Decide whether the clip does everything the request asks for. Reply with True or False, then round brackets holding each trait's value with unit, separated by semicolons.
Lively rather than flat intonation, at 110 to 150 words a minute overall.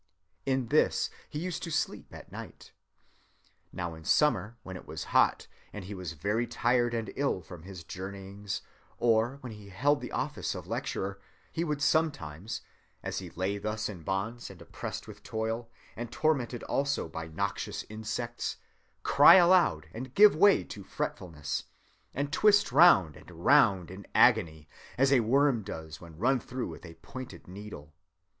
False (6.3 semitones; 165 wpm)